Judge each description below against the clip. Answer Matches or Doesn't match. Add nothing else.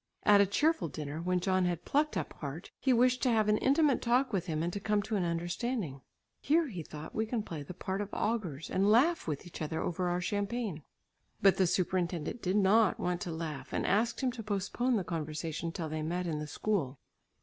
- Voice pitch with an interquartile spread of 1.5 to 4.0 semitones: Doesn't match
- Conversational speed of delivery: Doesn't match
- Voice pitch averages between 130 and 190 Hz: Matches